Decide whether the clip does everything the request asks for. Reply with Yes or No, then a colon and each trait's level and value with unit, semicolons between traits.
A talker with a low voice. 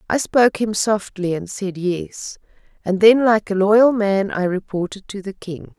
No: high, 200 Hz